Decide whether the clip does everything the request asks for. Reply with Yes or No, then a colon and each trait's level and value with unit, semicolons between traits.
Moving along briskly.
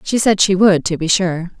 Yes: fast, 265 wpm